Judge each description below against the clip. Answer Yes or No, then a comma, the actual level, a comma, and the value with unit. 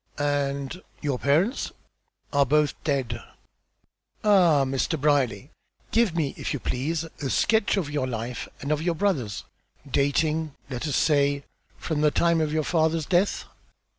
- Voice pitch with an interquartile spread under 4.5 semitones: Yes, average, 2.9 semitones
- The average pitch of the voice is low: No, medium, 150 Hz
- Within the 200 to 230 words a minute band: No, average, 145 wpm